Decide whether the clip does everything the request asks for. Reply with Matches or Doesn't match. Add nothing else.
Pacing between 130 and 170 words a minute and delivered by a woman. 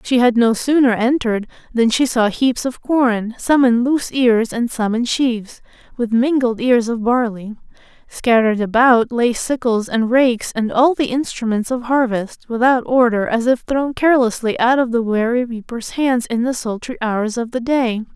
Doesn't match